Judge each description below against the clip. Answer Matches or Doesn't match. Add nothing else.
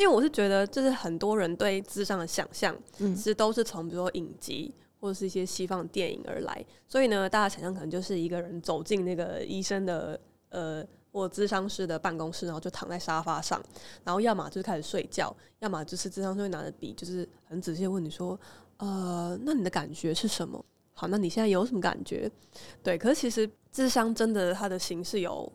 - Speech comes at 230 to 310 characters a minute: Doesn't match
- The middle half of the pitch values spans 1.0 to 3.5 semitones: Matches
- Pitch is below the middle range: Doesn't match